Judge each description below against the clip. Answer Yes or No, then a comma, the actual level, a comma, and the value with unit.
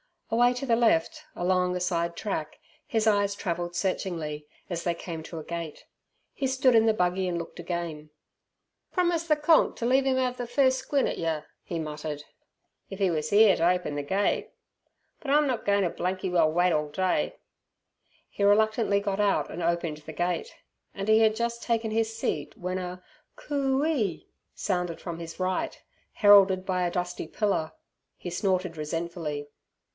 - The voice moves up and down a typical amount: Yes, average, 4.7 semitones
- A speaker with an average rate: Yes, average, 175 wpm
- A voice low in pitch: No, medium, 185 Hz